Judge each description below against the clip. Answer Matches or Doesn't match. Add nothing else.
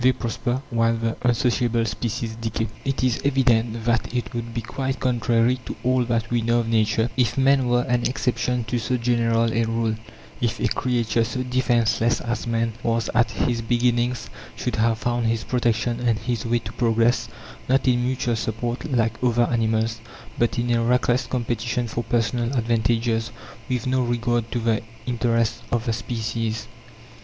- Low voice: Matches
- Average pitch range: Doesn't match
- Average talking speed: Matches